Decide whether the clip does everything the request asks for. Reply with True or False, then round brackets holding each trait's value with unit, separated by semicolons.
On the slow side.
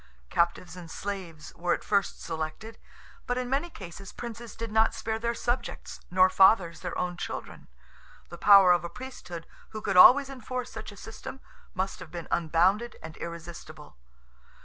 False (165 wpm)